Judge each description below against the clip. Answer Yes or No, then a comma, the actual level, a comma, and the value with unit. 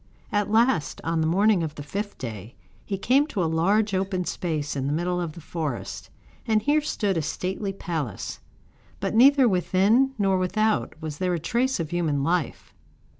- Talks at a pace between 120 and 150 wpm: No, average, 180 wpm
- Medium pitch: Yes, medium, 180 Hz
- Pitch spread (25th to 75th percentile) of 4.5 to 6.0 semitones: Yes, average, 4.9 semitones